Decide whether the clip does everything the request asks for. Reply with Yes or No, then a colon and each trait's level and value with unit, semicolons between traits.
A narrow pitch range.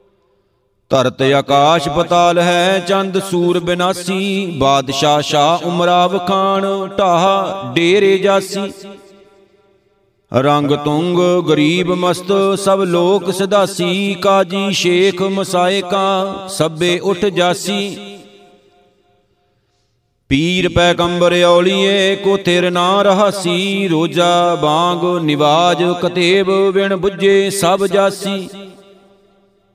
Yes: narrow, 2.0 semitones